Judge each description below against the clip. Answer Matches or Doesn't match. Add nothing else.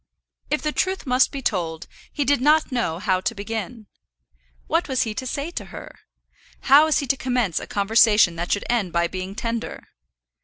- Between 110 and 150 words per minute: Doesn't match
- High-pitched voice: Matches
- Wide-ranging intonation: Matches